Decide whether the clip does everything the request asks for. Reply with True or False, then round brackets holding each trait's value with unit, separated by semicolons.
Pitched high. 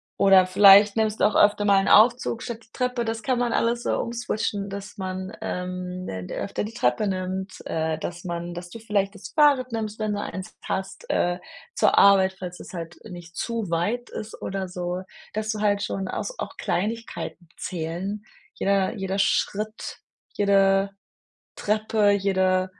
True (200 Hz)